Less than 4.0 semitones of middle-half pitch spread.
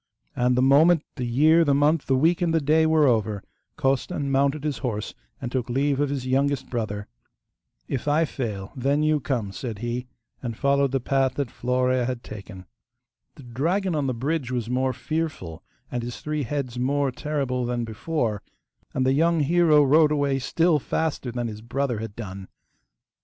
Yes: average, 3.6 semitones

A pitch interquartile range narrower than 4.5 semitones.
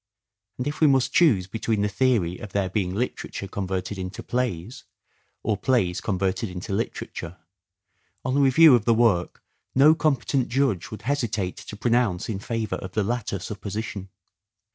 No: average, 4.9 semitones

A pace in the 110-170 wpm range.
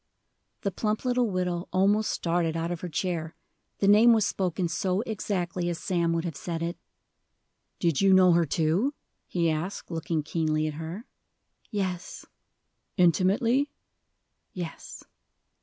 Yes: average, 140 wpm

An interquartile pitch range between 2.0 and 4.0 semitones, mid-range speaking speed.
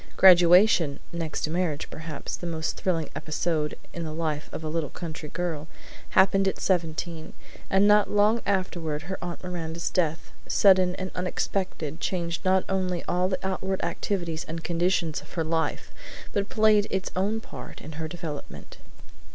Yes: average, 2.9 semitones; average, 160 wpm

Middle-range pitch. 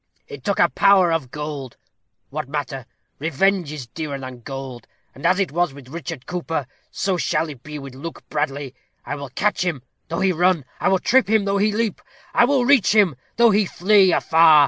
Yes: medium, 165 Hz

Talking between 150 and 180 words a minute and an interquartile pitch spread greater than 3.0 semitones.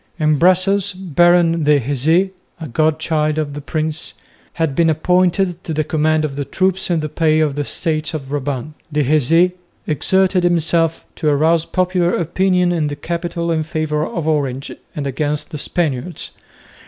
No: average, 165 wpm; narrow, 2.5 semitones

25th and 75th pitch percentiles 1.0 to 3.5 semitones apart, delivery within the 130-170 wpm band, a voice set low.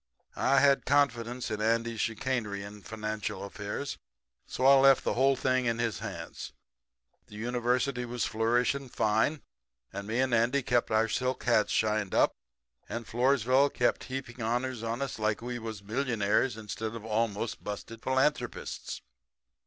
Yes: average, 2.9 semitones; average, 155 wpm; low, 115 Hz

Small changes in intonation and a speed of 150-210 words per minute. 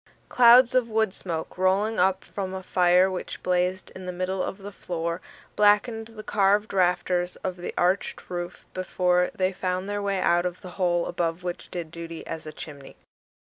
Yes: narrow, 2.0 semitones; average, 180 wpm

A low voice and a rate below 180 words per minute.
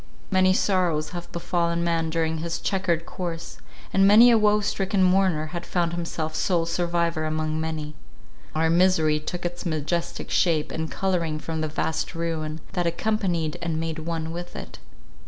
No: medium, 170 Hz; average, 160 wpm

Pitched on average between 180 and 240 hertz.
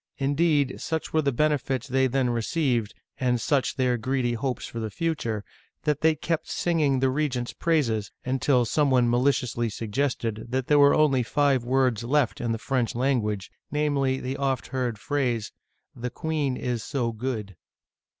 No: low, 130 Hz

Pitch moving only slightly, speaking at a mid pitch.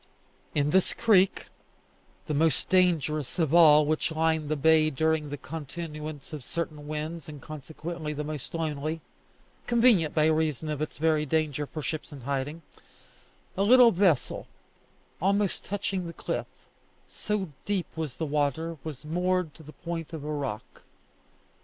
Yes: narrow, 2.1 semitones; medium, 155 Hz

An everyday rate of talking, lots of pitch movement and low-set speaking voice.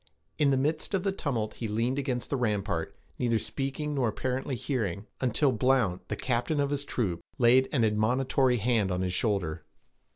No: average, 175 wpm; average, 4.1 semitones; low, 125 Hz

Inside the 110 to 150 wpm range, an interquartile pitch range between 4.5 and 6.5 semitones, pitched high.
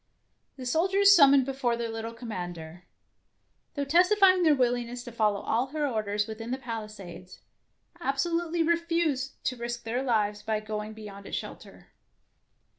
Yes: average, 145 wpm; average, 5.2 semitones; high, 240 Hz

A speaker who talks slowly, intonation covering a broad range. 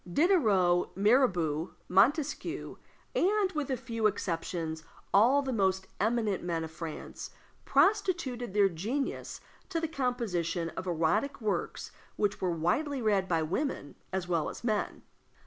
Yes: slow, 130 wpm; wide, 7.4 semitones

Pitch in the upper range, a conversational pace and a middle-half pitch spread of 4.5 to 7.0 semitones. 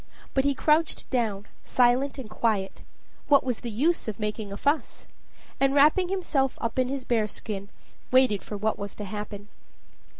Yes: high, 245 Hz; average, 170 wpm; average, 4.8 semitones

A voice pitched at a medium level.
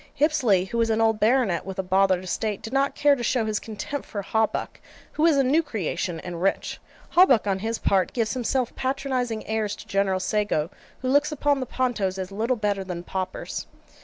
No: high, 220 Hz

